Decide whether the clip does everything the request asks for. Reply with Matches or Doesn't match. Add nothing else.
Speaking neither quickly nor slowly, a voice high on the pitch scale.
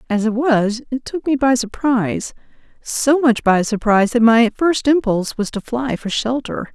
Matches